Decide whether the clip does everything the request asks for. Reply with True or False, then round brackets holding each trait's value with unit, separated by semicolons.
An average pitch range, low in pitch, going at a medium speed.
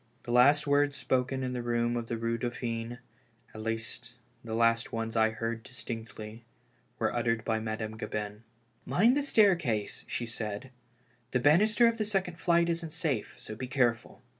True (4.0 semitones; 120 Hz; 175 wpm)